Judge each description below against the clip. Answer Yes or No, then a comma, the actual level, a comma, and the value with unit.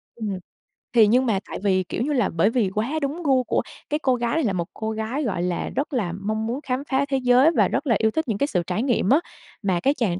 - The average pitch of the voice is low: No, high, 235 Hz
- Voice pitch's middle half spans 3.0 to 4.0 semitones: No, average, 4.9 semitones